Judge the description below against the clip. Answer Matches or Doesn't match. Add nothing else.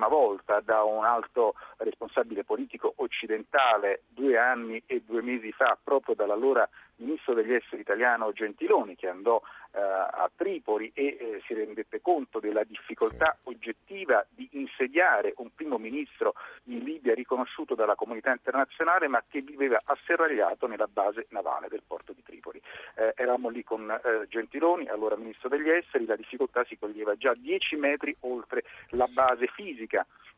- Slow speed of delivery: Doesn't match